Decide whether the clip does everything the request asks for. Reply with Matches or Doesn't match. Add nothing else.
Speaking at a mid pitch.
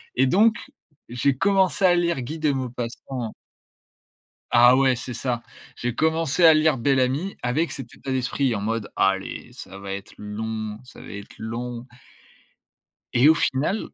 Doesn't match